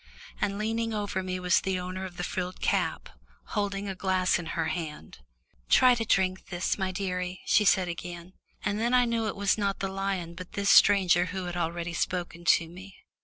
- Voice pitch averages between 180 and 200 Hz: Yes, medium, 185 Hz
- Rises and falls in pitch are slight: Yes, narrow, 2.2 semitones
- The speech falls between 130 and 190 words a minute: No, average, 200 wpm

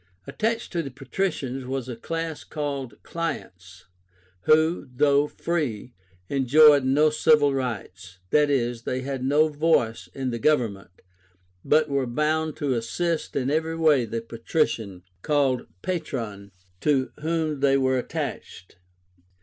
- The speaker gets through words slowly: Yes, slow, 130 wpm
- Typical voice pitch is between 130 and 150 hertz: Yes, medium, 140 Hz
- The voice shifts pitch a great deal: No, average, 4.1 semitones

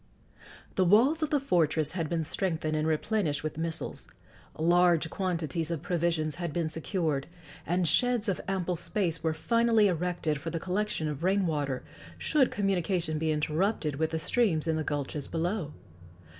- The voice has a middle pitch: Yes, medium, 170 Hz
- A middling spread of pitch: Yes, average, 3.4 semitones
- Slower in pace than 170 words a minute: Yes, average, 160 wpm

